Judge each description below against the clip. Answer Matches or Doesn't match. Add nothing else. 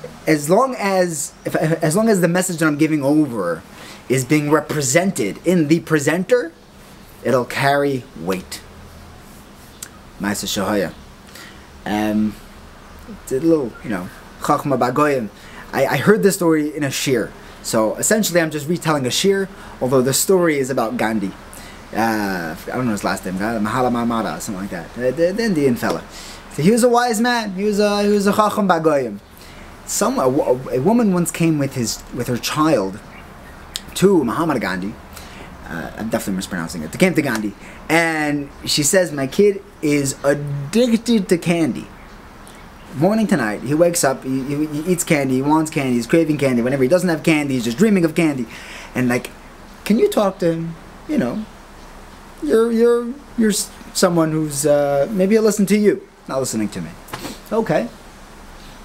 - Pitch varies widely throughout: Matches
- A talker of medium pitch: Matches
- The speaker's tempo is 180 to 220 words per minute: Doesn't match